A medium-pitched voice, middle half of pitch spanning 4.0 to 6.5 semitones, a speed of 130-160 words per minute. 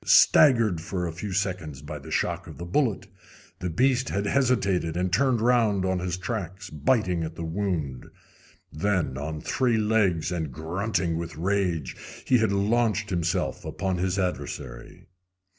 No: very low, 95 Hz; average, 4.3 semitones; average, 155 wpm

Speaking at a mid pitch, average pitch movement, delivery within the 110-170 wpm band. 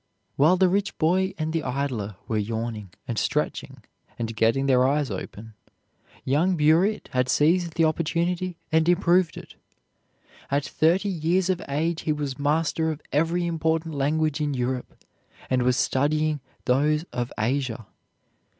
Yes: medium, 150 Hz; average, 4.4 semitones; average, 145 wpm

